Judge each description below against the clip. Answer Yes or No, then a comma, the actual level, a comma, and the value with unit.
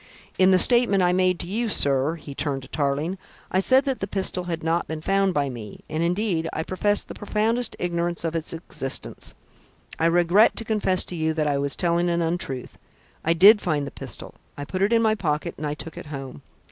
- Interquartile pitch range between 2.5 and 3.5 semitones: No, average, 4.1 semitones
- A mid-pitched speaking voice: Yes, medium, 170 Hz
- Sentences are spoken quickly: Yes, fast, 220 wpm